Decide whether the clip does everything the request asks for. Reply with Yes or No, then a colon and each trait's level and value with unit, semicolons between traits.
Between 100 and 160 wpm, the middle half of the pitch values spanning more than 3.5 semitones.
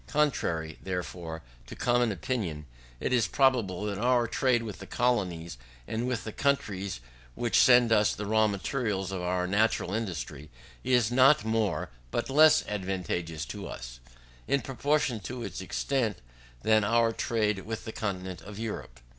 Yes: average, 155 wpm; average, 4.7 semitones